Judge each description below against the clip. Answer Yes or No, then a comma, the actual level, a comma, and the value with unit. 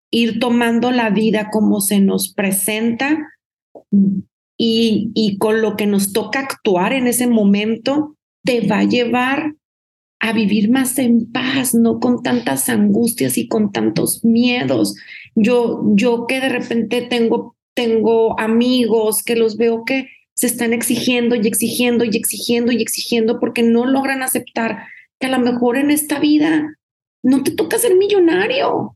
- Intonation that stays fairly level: Yes, narrow, 2.3 semitones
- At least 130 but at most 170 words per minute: Yes, average, 150 wpm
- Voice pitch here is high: Yes, high, 235 Hz